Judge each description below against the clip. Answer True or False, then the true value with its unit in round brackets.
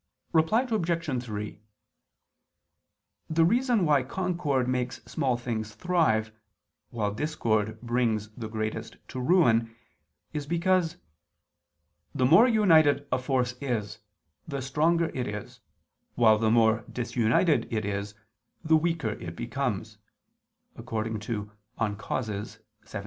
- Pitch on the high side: False (125 Hz)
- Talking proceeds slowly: True (110 wpm)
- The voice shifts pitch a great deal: True (6.6 semitones)